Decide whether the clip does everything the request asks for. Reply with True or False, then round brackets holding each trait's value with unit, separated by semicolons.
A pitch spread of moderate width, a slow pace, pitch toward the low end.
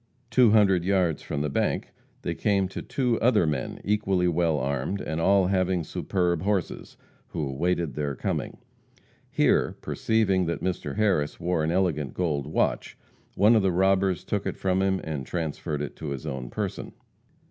False (4.1 semitones; 170 wpm; 90 Hz)